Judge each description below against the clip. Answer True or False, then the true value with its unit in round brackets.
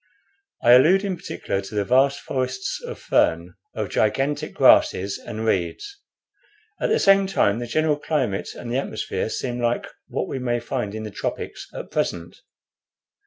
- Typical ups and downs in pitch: False (5.8 semitones)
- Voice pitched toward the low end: True (120 Hz)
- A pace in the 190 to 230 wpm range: False (165 wpm)